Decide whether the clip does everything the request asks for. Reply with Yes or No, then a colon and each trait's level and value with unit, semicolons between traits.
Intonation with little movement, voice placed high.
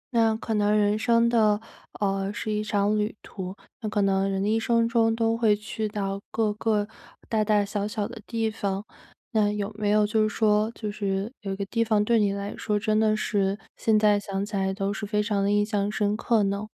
Yes: narrow, 1.4 semitones; high, 210 Hz